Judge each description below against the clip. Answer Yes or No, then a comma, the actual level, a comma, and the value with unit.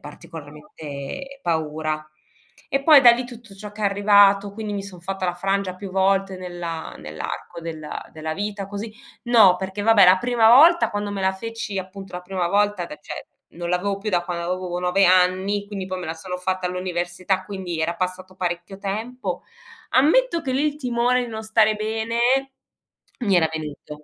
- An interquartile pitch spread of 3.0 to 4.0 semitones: Yes, average, 3.3 semitones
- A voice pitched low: No, high, 190 Hz